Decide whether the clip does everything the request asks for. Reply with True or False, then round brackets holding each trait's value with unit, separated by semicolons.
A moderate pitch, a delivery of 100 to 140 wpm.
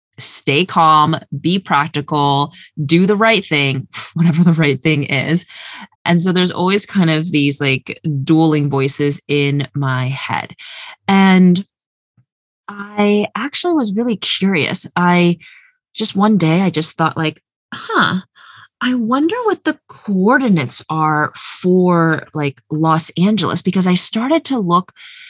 True (175 Hz; 135 wpm)